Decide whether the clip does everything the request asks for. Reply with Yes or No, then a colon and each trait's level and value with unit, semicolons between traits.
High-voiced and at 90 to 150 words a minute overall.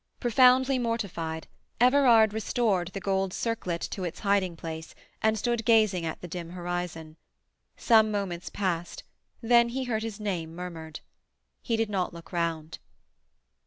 Yes: high, 195 Hz; average, 140 wpm